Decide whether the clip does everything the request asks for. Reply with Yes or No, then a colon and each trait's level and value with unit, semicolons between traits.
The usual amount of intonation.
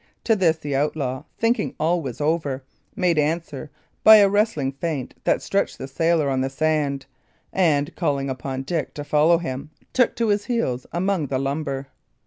Yes: average, 4.0 semitones